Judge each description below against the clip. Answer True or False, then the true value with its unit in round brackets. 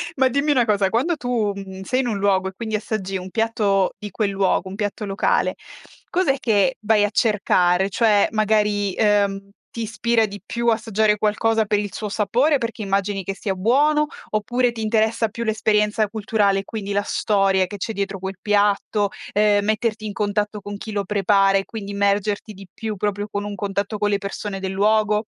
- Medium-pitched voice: False (210 Hz)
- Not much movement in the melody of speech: True (1.9 semitones)